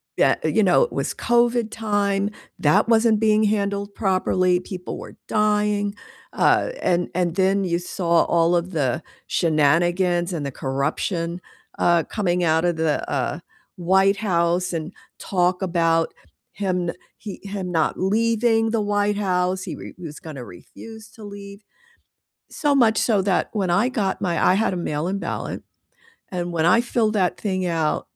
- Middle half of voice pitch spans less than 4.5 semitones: Yes, average, 3.4 semitones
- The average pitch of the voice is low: No, medium, 185 Hz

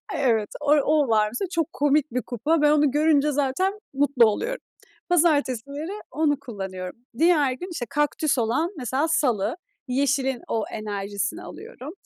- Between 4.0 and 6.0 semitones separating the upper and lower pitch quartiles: Yes, average, 4.4 semitones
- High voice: Yes, very high, 280 Hz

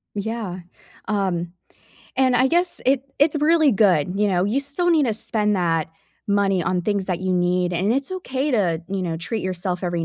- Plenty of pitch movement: Yes, wide, 6.5 semitones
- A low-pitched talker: No, high, 200 Hz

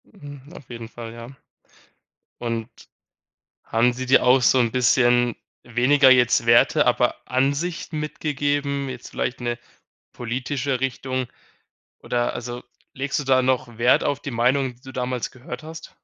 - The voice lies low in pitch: Yes, low, 130 Hz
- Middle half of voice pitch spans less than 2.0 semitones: No, narrow, 2.5 semitones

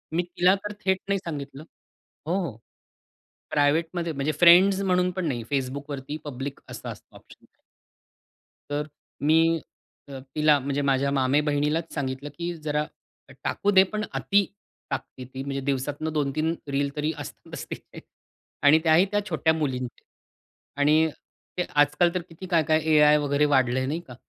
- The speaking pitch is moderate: Yes, medium, 150 Hz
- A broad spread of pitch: No, average, 3.4 semitones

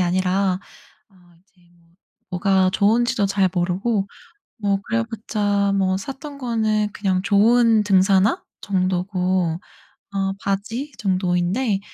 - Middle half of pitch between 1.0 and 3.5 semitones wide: Yes, narrow, 2.6 semitones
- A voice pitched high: Yes, high, 195 Hz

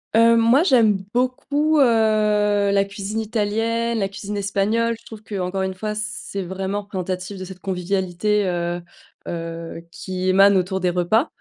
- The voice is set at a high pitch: Yes, high, 200 Hz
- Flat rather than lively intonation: No, average, 3.1 semitones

